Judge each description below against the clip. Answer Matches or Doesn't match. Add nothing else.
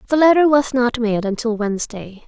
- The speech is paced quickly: Doesn't match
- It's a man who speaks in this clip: Doesn't match